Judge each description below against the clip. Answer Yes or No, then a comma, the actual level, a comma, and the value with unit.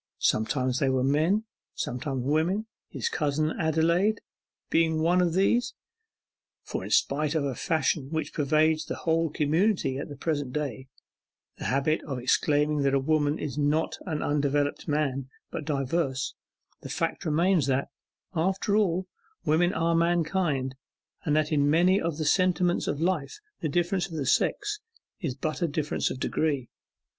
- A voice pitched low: No, medium, 155 Hz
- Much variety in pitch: No, average, 3.2 semitones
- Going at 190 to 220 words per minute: No, average, 150 wpm